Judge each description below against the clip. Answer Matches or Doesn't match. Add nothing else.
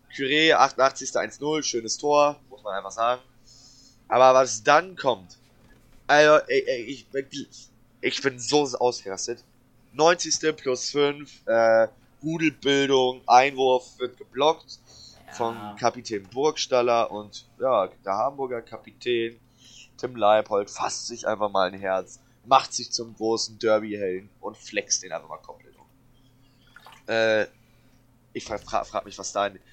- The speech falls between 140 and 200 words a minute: Doesn't match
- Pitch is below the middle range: Matches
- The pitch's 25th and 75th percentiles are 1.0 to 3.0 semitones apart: Matches